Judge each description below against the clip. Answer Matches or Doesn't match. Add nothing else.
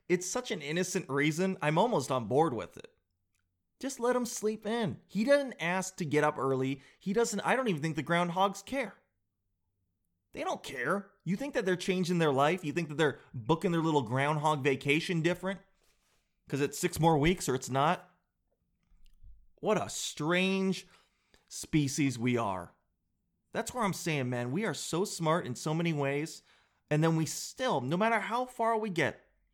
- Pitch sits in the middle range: Matches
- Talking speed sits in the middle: Matches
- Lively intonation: Matches